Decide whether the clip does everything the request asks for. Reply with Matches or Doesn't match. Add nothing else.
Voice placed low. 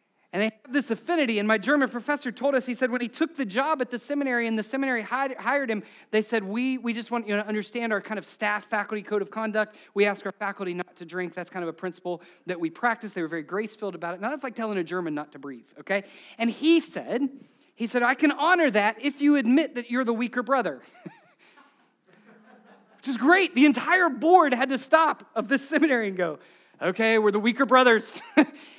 Doesn't match